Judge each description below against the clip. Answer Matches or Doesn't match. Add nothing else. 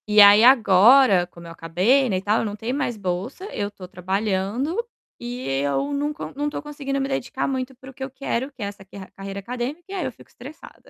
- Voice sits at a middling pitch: Doesn't match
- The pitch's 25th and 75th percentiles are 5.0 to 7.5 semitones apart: Matches